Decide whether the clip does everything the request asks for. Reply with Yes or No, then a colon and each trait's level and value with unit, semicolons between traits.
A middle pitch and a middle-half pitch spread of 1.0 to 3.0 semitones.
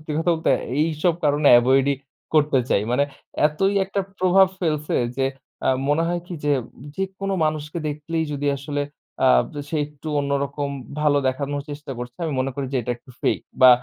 Yes: medium, 145 Hz; narrow, 2.4 semitones